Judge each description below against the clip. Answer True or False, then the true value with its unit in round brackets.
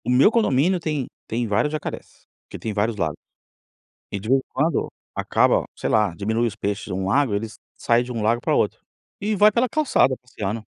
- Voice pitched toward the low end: True (120 Hz)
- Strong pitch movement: True (6.0 semitones)